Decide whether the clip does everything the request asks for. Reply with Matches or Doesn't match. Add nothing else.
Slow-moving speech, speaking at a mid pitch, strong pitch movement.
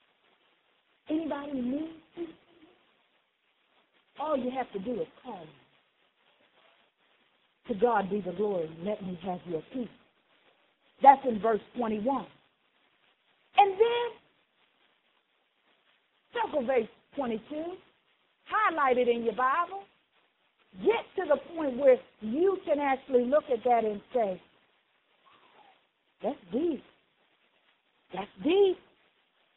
Doesn't match